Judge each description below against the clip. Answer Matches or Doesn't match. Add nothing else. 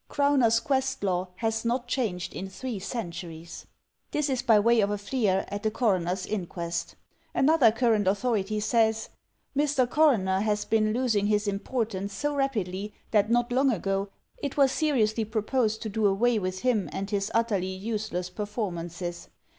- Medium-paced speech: Matches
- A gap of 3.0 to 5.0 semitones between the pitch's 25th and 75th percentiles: Matches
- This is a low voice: Doesn't match